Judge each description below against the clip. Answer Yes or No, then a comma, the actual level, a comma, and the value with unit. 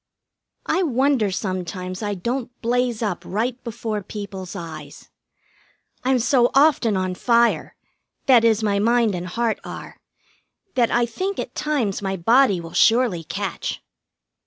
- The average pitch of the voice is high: Yes, high, 225 Hz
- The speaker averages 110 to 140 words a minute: Yes, slow, 135 wpm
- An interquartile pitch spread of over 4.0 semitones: Yes, average, 4.4 semitones